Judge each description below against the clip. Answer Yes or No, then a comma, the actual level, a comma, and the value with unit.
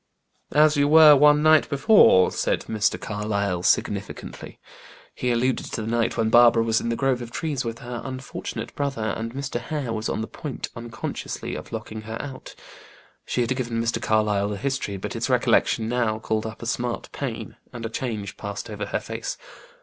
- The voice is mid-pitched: No, low, 115 Hz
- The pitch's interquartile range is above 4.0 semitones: No, average, 3.3 semitones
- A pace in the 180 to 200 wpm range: Yes, average, 190 wpm